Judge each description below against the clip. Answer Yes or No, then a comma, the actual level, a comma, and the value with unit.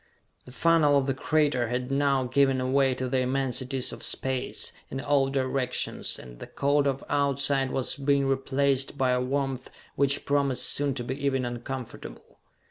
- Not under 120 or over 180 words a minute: Yes, average, 165 wpm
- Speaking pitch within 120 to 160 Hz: Yes, low, 135 Hz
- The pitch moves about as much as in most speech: No, narrow, 1.5 semitones